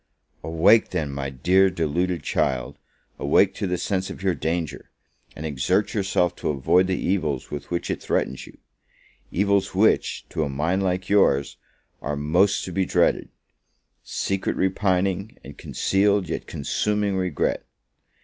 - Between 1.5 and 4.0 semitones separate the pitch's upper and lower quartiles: No, average, 4.4 semitones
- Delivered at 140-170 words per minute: Yes, average, 150 wpm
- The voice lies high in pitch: No, very low, 90 Hz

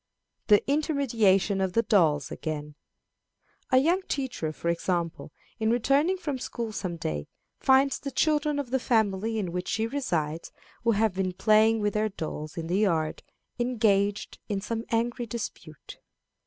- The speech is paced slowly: No, average, 155 wpm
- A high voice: Yes, high, 215 Hz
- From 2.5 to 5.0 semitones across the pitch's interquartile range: No, wide, 5.6 semitones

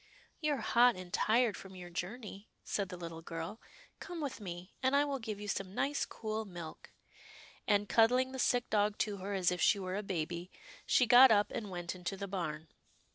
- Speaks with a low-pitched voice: No, high, 205 Hz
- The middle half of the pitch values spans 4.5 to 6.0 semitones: Yes, average, 5.0 semitones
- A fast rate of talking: Yes, fast, 210 wpm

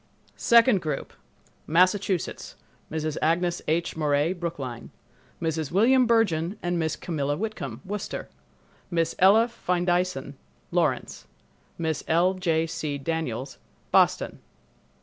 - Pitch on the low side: No, medium, 170 Hz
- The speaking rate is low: Yes, slow, 100 wpm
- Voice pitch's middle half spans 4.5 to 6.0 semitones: No, average, 3.0 semitones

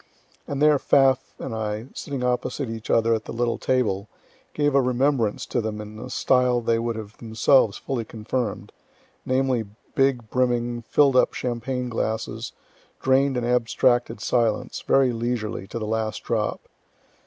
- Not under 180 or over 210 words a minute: No, average, 155 wpm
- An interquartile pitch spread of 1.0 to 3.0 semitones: Yes, average, 2.7 semitones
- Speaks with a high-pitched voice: No, low, 120 Hz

